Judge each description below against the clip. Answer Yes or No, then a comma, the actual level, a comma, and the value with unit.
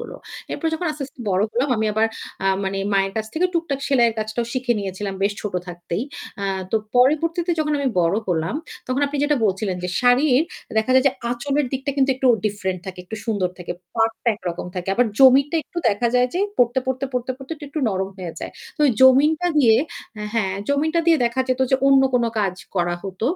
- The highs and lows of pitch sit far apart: Yes, wide, 5.8 semitones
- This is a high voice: Yes, high, 245 Hz